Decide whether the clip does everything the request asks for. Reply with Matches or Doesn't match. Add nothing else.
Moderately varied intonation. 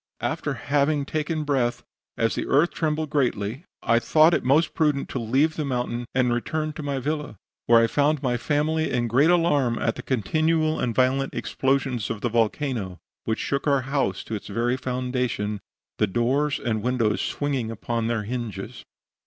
Matches